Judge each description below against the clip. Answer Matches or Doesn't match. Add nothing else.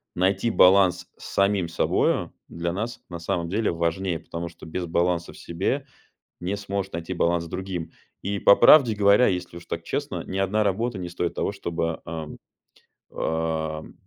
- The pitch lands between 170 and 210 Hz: Doesn't match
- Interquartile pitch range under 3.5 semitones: Matches